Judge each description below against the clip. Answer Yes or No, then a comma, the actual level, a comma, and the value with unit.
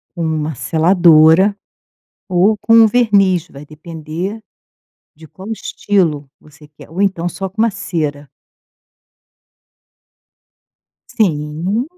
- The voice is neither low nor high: Yes, medium, 175 Hz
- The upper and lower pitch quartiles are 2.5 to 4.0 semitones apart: No, average, 4.4 semitones